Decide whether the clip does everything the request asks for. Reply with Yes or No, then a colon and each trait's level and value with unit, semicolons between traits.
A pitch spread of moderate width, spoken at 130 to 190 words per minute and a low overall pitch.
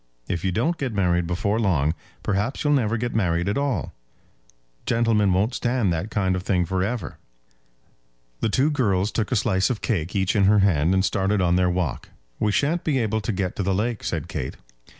No: average, 4.0 semitones; fast, 205 wpm; low, 100 Hz